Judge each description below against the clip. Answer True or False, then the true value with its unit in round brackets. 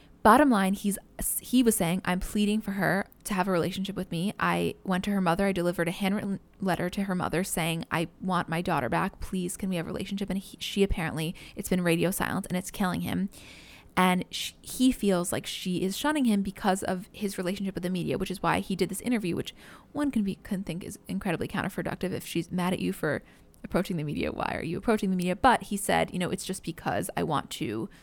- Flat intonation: True (2.3 semitones)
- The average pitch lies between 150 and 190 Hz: True (185 Hz)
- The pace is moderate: False (240 wpm)